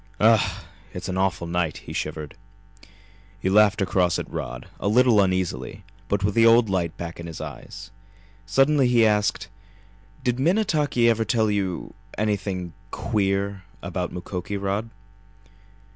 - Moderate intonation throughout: Yes, average, 3.7 semitones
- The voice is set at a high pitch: No, low, 100 Hz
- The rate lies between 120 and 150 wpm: Yes, average, 140 wpm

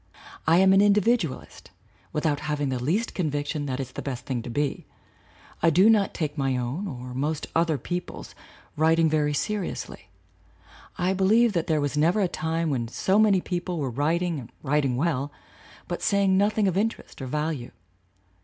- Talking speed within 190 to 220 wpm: No, average, 180 wpm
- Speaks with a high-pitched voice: No, medium, 160 Hz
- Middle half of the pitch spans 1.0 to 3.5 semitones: No, average, 5.0 semitones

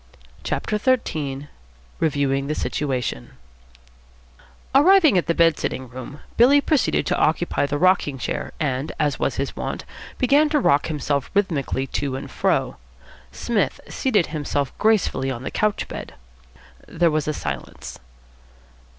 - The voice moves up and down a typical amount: No, wide, 7.2 semitones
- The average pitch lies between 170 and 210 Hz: No, medium, 150 Hz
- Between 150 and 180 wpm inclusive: No, slow, 135 wpm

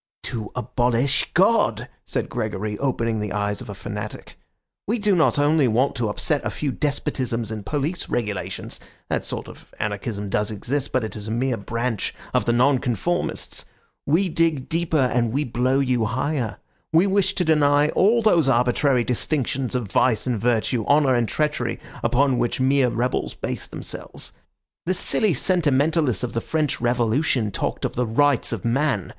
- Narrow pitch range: No, average, 4.4 semitones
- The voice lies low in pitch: Yes, low, 125 Hz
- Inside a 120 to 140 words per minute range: No, average, 165 wpm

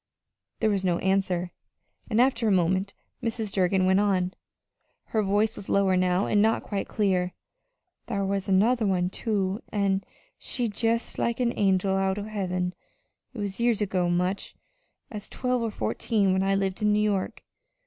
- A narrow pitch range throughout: Yes, narrow, 2.3 semitones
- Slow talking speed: No, average, 170 wpm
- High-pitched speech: Yes, high, 195 Hz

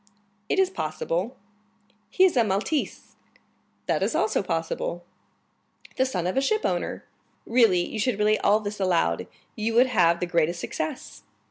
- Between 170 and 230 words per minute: No, average, 150 wpm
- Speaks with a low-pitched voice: No, high, 215 Hz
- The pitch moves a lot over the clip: Yes, wide, 6.6 semitones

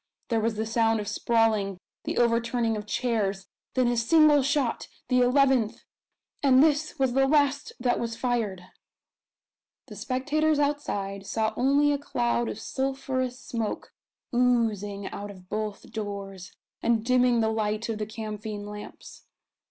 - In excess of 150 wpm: No, average, 145 wpm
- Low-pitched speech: No, high, 230 Hz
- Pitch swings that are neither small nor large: Yes, average, 3.6 semitones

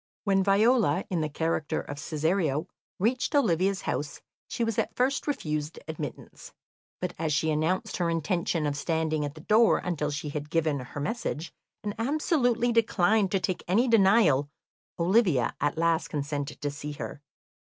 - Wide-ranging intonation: Yes, wide, 5.8 semitones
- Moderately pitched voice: Yes, medium, 165 Hz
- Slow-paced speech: No, average, 160 wpm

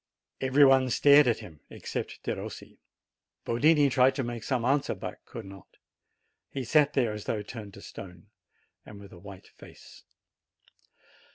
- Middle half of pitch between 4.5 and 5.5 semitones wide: Yes, average, 5.2 semitones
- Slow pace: No, average, 155 wpm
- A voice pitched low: Yes, low, 120 Hz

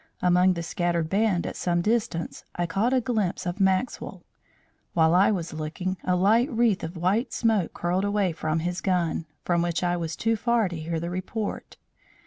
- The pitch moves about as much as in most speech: Yes, average, 3.5 semitones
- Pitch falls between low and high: Yes, medium, 180 Hz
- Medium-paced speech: Yes, average, 185 wpm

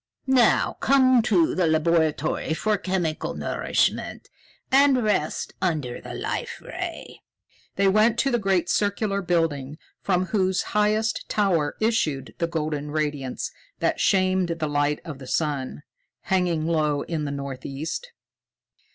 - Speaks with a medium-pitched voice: Yes, medium, 170 Hz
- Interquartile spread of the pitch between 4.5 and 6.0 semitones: Yes, average, 5.2 semitones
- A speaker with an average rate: No, slow, 130 wpm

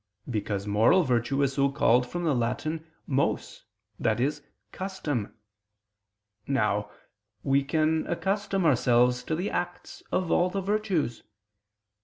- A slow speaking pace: Yes, slow, 120 wpm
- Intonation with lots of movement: Yes, wide, 6.4 semitones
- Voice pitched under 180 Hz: Yes, medium, 140 Hz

